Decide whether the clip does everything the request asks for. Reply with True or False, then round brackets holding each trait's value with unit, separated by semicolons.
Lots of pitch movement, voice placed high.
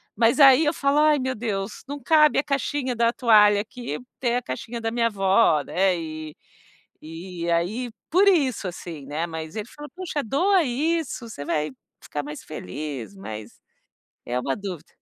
True (9.0 semitones; 220 Hz)